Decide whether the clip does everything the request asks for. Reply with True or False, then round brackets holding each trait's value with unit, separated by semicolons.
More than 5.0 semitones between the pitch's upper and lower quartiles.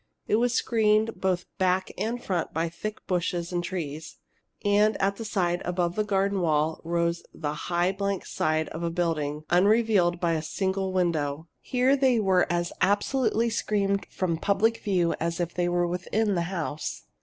False (3.2 semitones)